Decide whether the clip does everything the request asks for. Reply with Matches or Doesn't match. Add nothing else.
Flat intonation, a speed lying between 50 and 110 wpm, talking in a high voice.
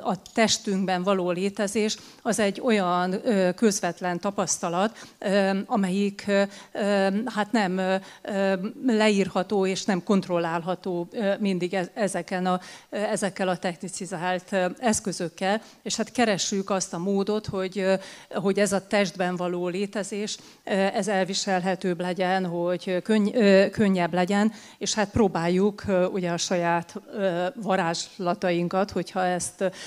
Matches